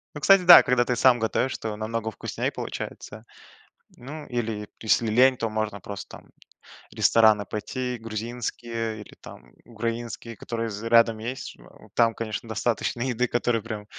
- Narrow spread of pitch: Yes, narrow, 2.0 semitones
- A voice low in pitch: Yes, low, 115 Hz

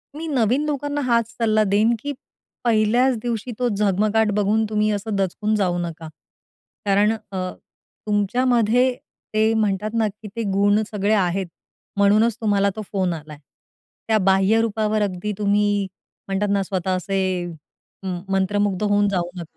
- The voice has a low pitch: No, high, 210 Hz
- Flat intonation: Yes, narrow, 2.3 semitones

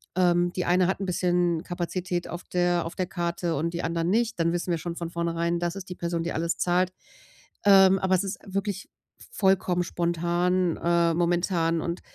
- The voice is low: No, medium, 175 Hz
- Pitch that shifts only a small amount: Yes, narrow, 1.4 semitones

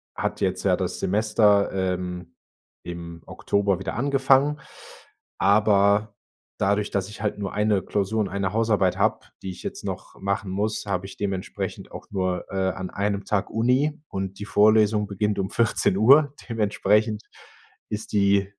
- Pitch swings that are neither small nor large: No, narrow, 1.9 semitones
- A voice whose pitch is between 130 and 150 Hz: No, low, 100 Hz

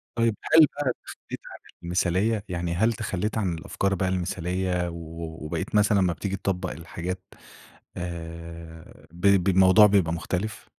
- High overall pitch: No, very low, 90 Hz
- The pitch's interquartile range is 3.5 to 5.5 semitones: No, average, 2.8 semitones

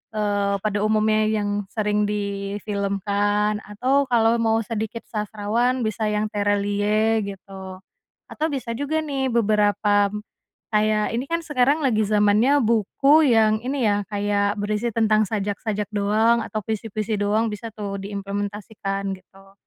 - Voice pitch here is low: No, high, 210 Hz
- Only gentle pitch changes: Yes, narrow, 1.8 semitones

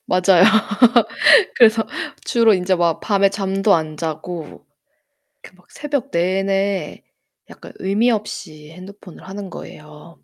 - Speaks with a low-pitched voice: No, high, 190 Hz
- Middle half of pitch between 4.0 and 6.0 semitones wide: No, average, 3.0 semitones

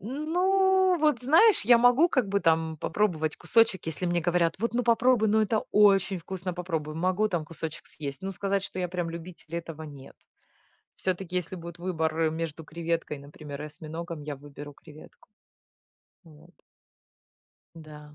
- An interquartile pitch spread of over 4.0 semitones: Yes, average, 5.0 semitones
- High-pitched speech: No, medium, 175 Hz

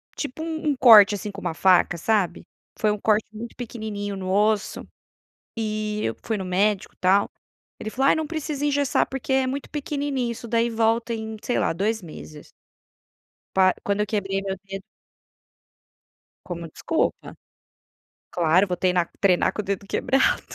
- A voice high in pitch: Yes, high, 215 Hz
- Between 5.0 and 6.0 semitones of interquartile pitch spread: No, average, 4.1 semitones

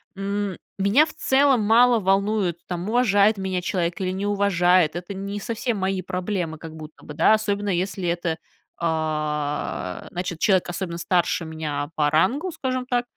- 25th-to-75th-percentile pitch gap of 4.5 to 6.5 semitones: No, average, 3.4 semitones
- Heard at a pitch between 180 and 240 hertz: Yes, high, 190 Hz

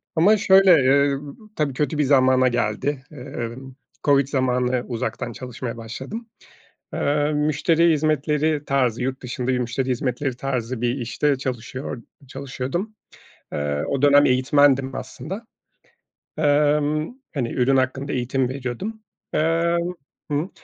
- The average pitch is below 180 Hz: Yes, low, 135 Hz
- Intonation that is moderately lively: Yes, average, 3.0 semitones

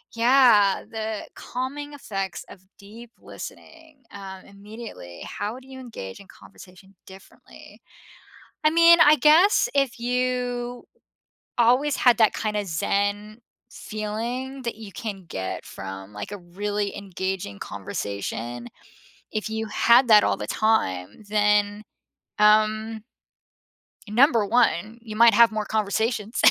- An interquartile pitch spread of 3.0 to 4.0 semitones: Yes, average, 3.6 semitones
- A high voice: Yes, high, 215 Hz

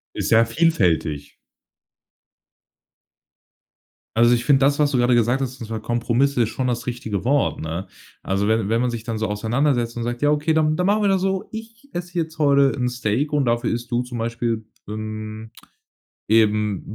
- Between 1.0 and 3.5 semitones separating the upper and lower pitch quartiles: No, average, 4.4 semitones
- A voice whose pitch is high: No, low, 120 Hz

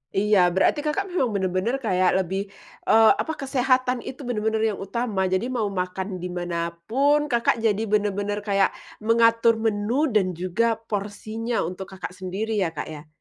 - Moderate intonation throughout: Yes, average, 3.6 semitones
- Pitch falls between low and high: No, high, 210 Hz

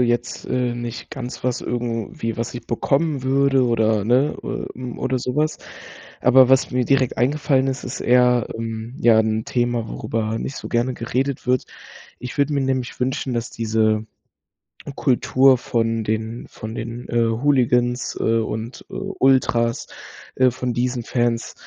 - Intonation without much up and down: Yes, narrow, 2.1 semitones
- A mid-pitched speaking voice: No, low, 120 Hz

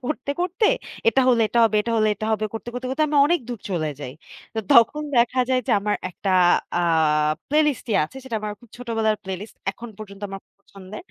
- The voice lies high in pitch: Yes, high, 230 Hz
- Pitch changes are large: No, average, 3.9 semitones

